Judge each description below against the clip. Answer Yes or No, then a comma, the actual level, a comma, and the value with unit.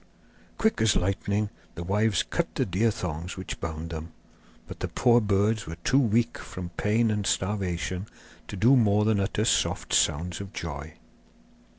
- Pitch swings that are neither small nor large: Yes, average, 4.0 semitones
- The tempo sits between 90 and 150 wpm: No, average, 165 wpm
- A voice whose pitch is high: No, low, 100 Hz